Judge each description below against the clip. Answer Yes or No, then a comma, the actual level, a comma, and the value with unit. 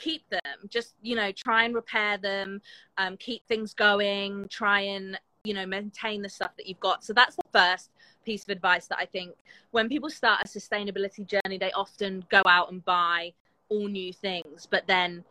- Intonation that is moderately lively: No, narrow, 2.3 semitones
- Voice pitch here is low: No, high, 200 Hz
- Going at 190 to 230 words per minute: Yes, fast, 205 wpm